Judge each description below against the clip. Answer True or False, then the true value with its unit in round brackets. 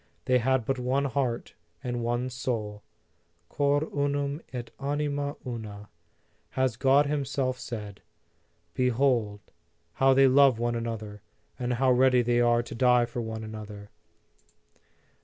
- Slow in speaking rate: True (130 wpm)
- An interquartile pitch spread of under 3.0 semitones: True (2.6 semitones)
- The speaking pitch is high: False (125 Hz)